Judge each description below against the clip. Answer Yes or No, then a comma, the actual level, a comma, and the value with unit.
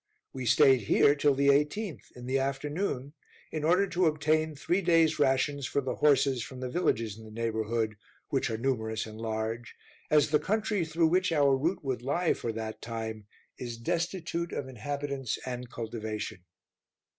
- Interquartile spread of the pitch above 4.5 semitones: Yes, average, 5.2 semitones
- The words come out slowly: No, average, 170 wpm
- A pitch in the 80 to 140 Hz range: Yes, low, 135 Hz